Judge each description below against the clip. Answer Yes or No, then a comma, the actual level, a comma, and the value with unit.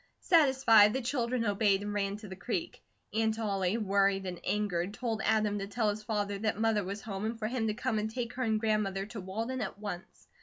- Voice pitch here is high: Yes, high, 215 Hz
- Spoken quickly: Yes, fast, 220 wpm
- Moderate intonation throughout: No, narrow, 2.2 semitones